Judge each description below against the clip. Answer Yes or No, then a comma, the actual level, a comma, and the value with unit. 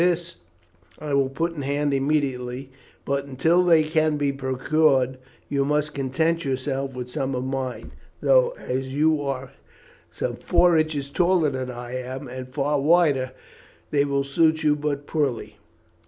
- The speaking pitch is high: No, medium, 140 Hz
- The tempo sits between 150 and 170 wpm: Yes, average, 155 wpm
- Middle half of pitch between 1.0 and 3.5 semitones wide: Yes, average, 2.9 semitones